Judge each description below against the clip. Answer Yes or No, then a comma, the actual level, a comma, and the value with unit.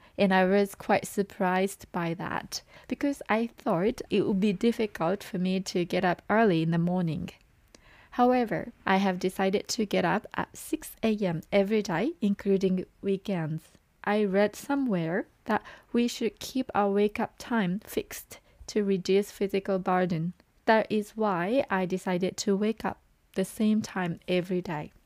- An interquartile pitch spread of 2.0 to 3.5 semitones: Yes, average, 2.7 semitones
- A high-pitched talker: Yes, high, 200 Hz